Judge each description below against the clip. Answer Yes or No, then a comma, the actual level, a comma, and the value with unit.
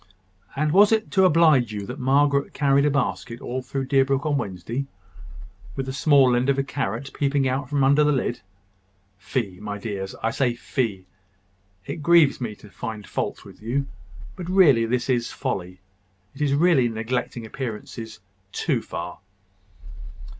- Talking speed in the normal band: Yes, average, 165 wpm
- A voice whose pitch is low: Yes, low, 130 Hz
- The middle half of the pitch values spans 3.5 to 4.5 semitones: Yes, average, 3.8 semitones